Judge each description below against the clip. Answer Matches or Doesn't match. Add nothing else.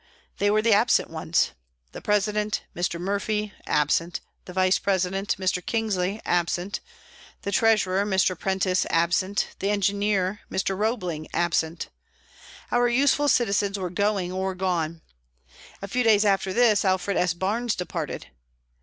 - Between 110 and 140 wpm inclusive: Matches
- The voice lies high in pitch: Matches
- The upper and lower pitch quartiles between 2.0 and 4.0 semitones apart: Matches